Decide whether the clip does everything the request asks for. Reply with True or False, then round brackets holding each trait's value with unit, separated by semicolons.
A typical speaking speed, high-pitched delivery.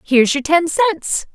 True (180 wpm; 315 Hz)